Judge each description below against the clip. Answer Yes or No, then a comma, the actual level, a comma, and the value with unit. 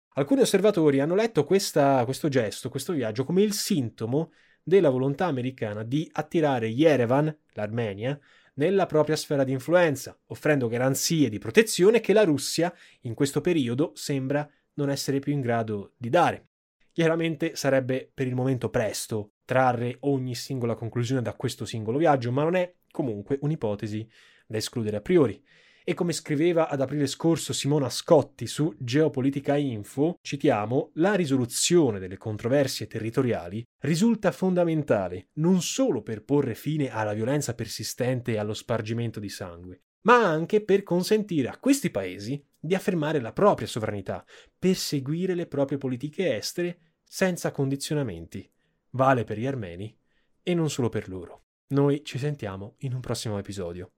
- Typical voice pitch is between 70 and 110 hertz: No, medium, 140 Hz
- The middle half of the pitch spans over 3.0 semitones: Yes, wide, 5.6 semitones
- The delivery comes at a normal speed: Yes, average, 145 wpm